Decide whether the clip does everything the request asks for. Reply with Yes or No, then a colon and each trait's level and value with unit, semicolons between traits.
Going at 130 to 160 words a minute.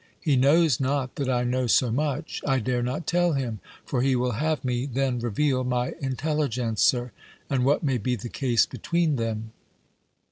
No: average, 175 wpm